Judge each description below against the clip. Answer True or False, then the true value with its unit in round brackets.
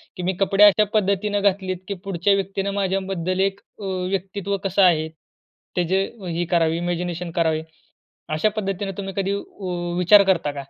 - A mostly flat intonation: True (2.1 semitones)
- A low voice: False (190 Hz)